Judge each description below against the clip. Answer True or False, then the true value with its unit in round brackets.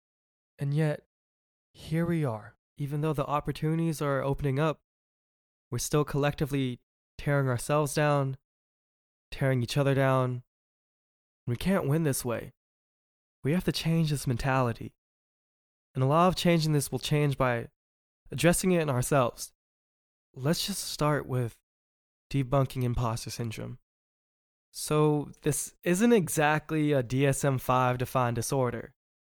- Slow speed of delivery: True (130 wpm)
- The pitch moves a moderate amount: True (4.0 semitones)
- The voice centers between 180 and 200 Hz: False (135 Hz)